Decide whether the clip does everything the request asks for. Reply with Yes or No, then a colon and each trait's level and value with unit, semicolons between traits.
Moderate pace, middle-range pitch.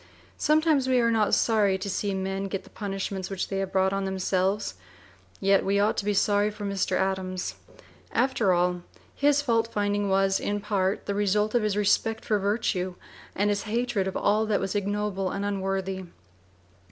No: average, 180 wpm; high, 200 Hz